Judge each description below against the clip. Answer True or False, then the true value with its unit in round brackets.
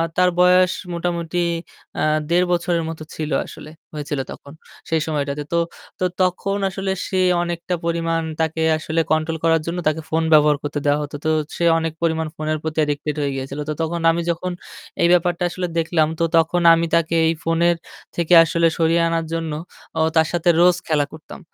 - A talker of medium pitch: True (165 Hz)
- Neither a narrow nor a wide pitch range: False (1.7 semitones)